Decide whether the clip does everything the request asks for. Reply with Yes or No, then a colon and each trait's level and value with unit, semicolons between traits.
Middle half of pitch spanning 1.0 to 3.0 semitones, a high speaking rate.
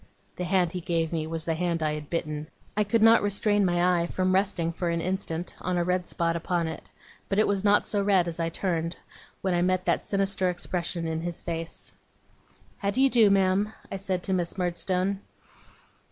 Yes: average, 2.7 semitones; fast, 210 wpm